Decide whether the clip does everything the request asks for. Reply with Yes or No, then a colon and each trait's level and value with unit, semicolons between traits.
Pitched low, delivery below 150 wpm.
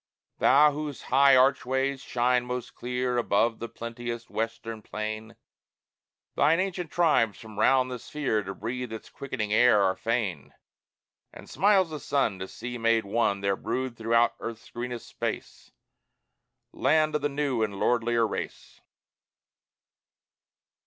Yes: low, 120 Hz; slow, 135 wpm